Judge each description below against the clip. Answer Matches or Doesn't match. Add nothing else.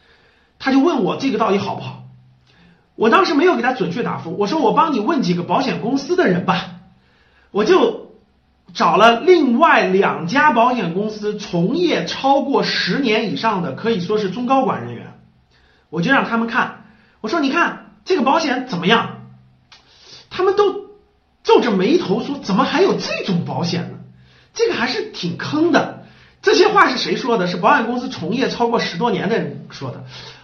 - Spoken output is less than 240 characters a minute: Doesn't match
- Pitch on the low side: Doesn't match